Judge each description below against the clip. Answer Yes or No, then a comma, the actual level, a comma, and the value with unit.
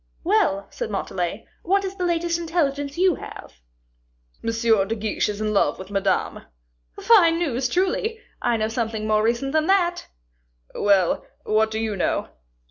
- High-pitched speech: Yes, high, 230 Hz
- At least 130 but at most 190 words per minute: Yes, average, 155 wpm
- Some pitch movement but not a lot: No, wide, 8.1 semitones